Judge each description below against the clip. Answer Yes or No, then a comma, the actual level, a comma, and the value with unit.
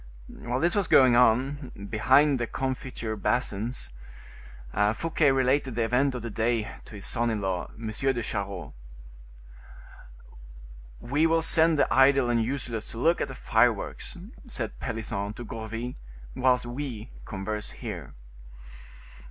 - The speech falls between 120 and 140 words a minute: Yes, slow, 135 wpm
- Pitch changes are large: No, average, 3.4 semitones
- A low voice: Yes, low, 120 Hz